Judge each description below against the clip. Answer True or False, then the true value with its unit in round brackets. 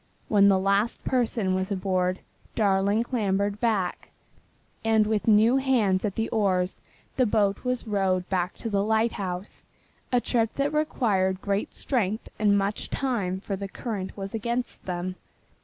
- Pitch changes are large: False (3.0 semitones)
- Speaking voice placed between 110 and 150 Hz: False (205 Hz)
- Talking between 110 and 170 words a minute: True (150 wpm)